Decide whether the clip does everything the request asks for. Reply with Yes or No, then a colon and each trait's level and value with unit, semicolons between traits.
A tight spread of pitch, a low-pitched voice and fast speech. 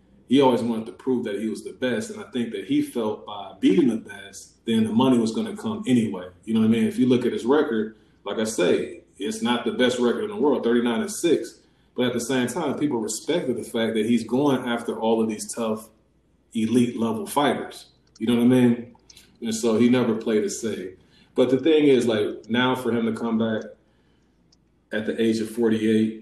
Yes: narrow, 2.2 semitones; low, 120 Hz; fast, 230 wpm